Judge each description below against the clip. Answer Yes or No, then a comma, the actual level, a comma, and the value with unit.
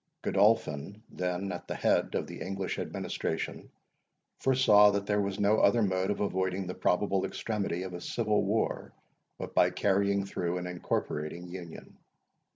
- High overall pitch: No, very low, 95 Hz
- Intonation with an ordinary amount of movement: No, narrow, 2.3 semitones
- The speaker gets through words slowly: No, average, 155 wpm